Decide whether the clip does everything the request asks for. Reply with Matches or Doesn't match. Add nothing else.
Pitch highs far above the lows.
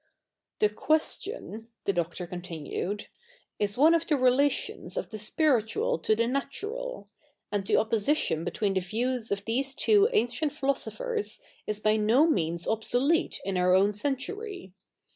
Matches